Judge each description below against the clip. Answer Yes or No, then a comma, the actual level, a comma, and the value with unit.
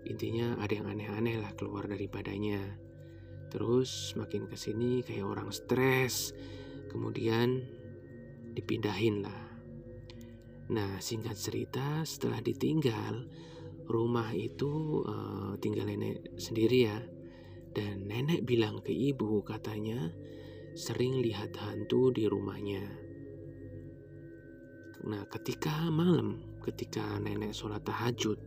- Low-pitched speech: Yes, low, 110 Hz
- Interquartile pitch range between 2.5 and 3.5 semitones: Yes, average, 3.0 semitones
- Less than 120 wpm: Yes, average, 100 wpm